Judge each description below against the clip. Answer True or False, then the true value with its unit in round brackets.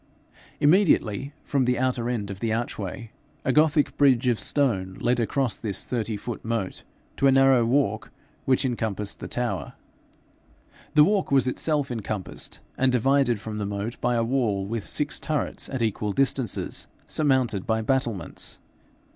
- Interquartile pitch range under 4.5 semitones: True (3.8 semitones)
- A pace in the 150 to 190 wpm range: True (155 wpm)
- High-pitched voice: False (120 Hz)